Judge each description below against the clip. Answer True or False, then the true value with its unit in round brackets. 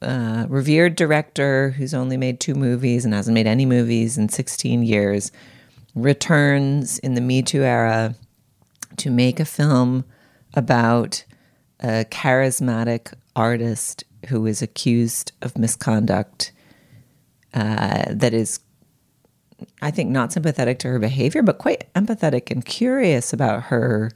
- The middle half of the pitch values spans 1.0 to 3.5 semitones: True (3.1 semitones)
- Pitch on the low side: True (125 Hz)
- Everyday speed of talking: False (130 wpm)